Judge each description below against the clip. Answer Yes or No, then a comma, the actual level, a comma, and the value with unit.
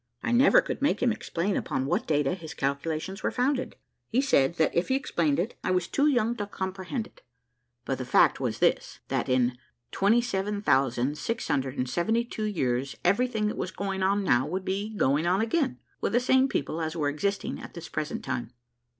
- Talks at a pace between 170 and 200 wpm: Yes, average, 185 wpm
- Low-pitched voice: No, high, 190 Hz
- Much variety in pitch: Yes, wide, 7.5 semitones